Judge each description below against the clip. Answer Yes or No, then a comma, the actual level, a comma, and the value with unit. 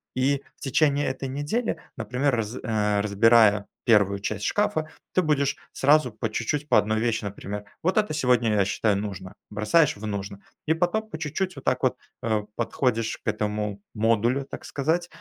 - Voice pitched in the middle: No, low, 120 Hz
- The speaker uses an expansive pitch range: Yes, wide, 5.7 semitones